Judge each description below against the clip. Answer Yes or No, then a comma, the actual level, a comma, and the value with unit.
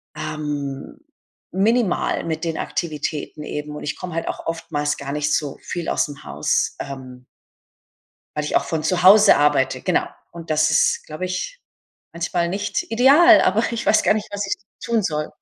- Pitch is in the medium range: Yes, medium, 160 Hz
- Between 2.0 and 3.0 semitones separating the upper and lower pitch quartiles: No, average, 4.7 semitones